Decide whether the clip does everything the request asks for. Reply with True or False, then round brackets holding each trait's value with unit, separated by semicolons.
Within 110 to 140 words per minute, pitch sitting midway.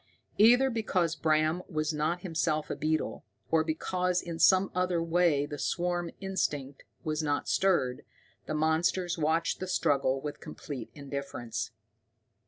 True (135 wpm; 160 Hz)